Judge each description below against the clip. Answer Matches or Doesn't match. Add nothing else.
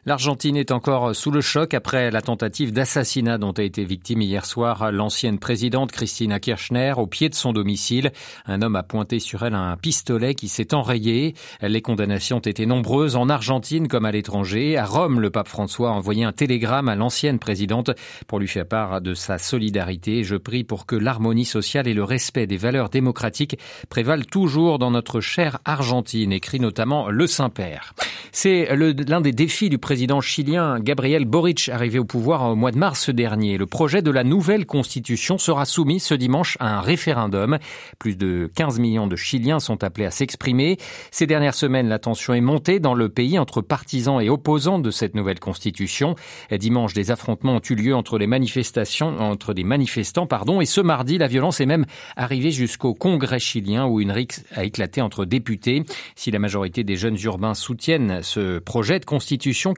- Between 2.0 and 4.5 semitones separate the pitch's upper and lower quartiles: Doesn't match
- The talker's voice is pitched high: Doesn't match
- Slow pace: Doesn't match